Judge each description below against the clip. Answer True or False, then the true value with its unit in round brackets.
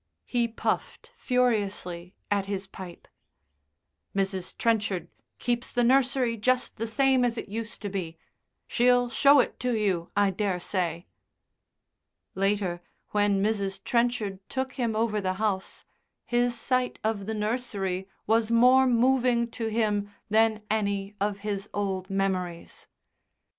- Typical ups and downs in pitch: True (3.6 semitones)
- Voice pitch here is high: True (215 Hz)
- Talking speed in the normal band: False (130 wpm)